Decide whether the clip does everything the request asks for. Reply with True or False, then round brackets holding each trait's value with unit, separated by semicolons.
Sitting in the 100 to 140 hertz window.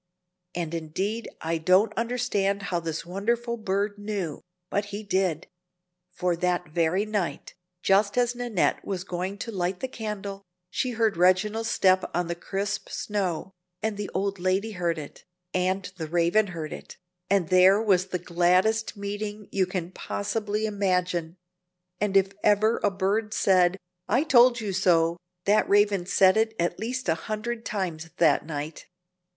False (195 Hz)